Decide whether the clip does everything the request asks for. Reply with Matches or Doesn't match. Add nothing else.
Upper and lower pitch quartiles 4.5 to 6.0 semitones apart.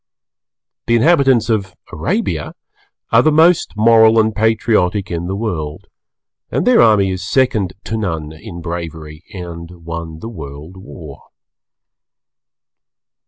Matches